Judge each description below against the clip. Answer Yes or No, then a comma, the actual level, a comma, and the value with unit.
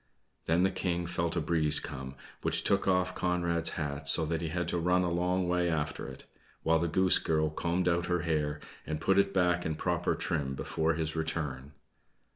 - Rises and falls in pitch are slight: Yes, narrow, 2.3 semitones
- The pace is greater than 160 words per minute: Yes, average, 200 wpm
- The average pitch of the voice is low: Yes, very low, 85 Hz